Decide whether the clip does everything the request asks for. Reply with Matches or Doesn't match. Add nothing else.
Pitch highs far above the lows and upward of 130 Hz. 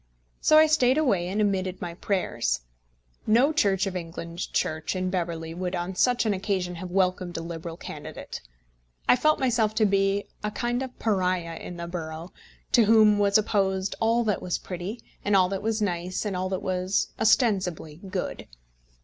Doesn't match